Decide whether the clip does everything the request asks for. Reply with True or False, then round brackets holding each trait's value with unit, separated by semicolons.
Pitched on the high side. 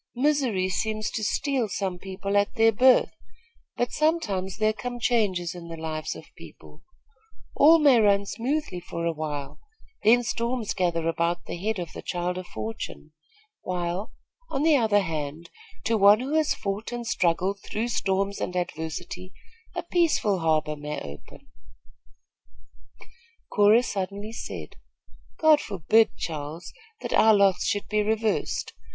True (200 Hz)